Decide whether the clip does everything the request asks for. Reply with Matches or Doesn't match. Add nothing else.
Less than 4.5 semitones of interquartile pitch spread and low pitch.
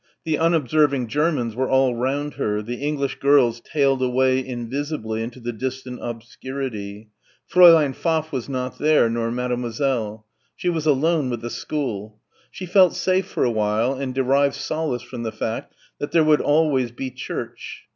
Matches